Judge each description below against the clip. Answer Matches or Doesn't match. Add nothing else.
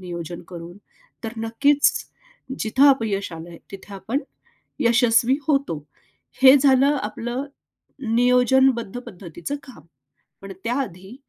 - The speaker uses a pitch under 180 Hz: Doesn't match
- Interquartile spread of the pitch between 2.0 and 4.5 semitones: Doesn't match